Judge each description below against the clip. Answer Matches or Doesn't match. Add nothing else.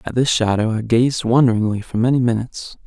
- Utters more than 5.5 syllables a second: Matches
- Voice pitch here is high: Doesn't match